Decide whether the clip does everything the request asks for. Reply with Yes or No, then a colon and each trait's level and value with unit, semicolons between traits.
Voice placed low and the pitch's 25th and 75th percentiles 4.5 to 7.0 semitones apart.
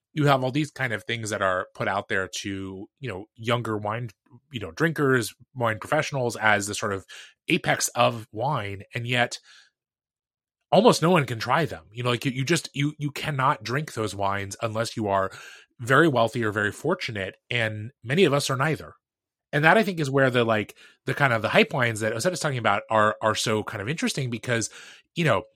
Yes: low, 120 Hz; average, 5.0 semitones